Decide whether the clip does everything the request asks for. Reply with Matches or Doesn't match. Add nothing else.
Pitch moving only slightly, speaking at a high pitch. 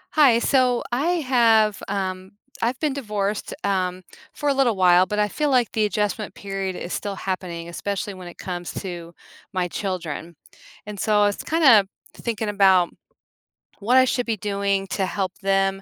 Doesn't match